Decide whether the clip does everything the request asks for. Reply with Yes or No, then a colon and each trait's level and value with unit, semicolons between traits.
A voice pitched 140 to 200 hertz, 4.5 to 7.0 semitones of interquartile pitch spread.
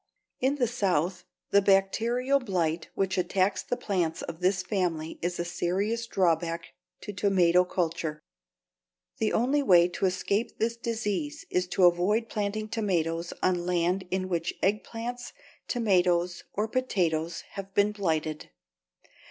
No: high, 190 Hz; average, 3.7 semitones